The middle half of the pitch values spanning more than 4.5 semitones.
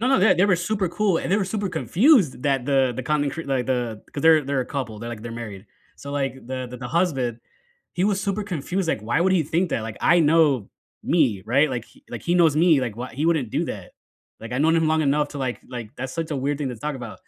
Yes: average, 5.3 semitones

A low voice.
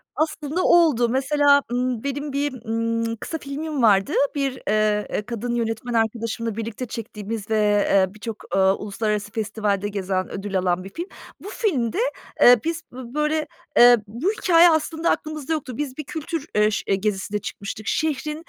No: high, 235 Hz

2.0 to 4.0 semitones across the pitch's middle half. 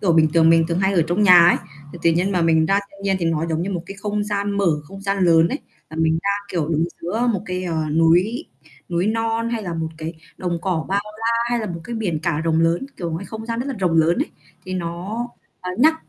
Yes: average, 3.6 semitones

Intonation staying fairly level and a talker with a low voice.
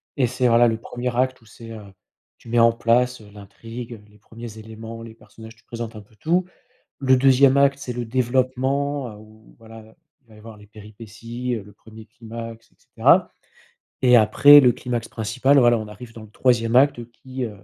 Yes: narrow, 2.2 semitones; low, 115 Hz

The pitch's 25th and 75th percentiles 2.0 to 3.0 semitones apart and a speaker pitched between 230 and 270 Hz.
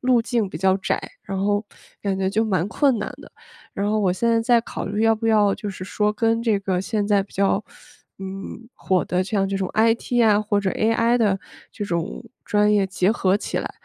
No: average, 2.7 semitones; high, 205 Hz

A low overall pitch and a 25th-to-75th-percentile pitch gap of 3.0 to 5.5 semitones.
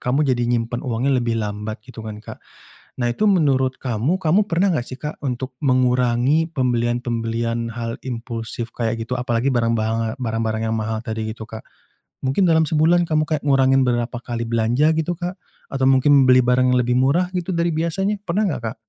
Yes: low, 125 Hz; average, 4.2 semitones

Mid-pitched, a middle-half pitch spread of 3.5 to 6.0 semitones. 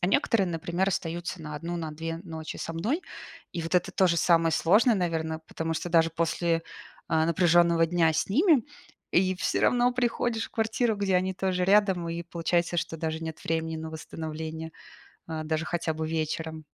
No: medium, 170 Hz; narrow, 2.6 semitones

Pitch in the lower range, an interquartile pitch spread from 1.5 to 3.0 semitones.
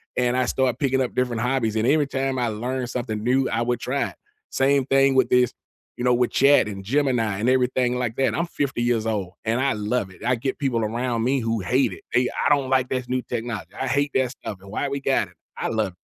Yes: low, 125 Hz; narrow, 2.6 semitones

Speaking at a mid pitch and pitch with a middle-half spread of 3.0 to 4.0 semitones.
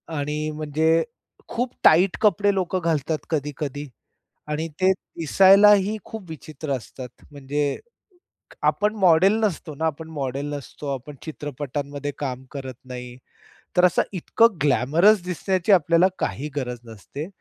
No: medium, 155 Hz; average, 4.5 semitones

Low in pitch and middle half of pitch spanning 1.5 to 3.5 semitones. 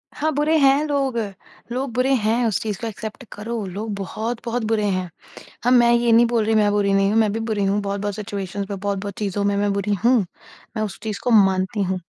No: high, 215 Hz; average, 2.8 semitones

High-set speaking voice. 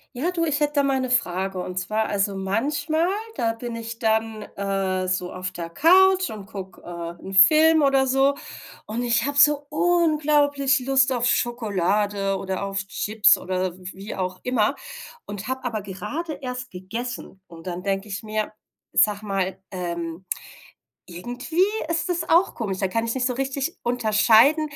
Yes: high, 225 Hz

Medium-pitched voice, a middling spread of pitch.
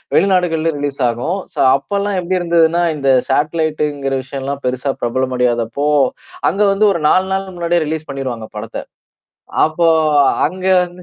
Yes: medium, 155 Hz; average, 4.5 semitones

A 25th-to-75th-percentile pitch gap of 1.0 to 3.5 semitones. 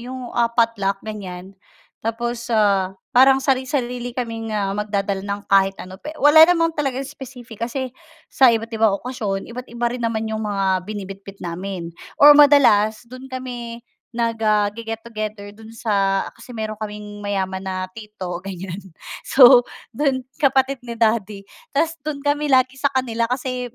No: average, 4.0 semitones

